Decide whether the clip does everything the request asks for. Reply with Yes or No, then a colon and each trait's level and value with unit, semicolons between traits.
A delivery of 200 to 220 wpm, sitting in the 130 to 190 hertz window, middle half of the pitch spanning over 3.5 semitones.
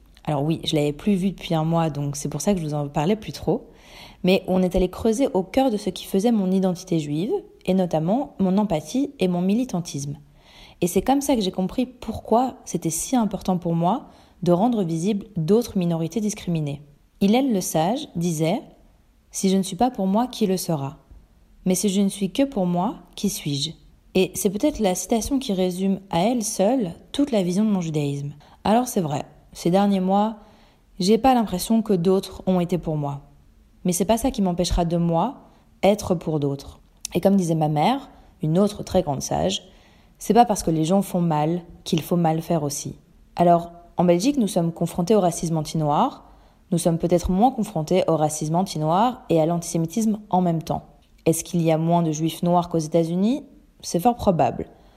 Yes: average, 205 wpm; medium, 185 Hz; average, 4.3 semitones